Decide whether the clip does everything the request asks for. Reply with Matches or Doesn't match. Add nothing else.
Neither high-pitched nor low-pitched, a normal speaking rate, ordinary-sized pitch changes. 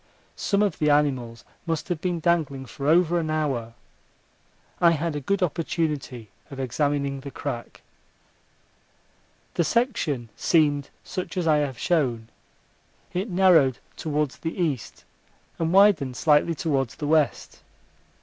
Doesn't match